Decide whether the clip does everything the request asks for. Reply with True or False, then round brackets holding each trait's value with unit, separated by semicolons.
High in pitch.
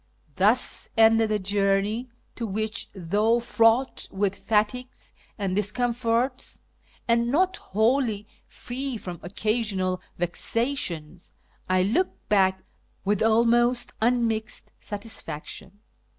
True (220 Hz)